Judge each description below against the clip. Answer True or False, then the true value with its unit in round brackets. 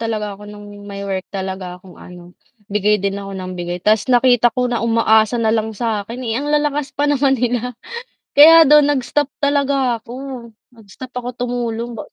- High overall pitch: True (230 Hz)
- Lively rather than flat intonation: False (4.1 semitones)